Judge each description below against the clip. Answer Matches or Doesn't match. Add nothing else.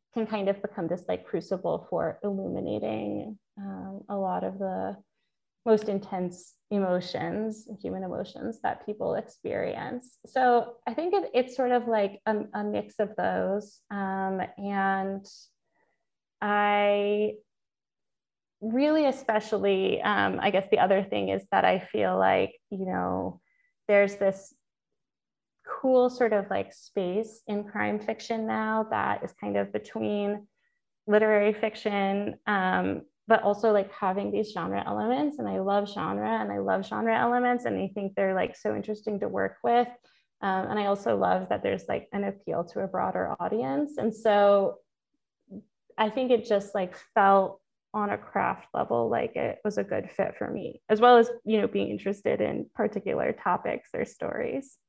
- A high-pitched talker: Matches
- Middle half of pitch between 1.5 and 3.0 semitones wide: Matches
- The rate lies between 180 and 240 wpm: Doesn't match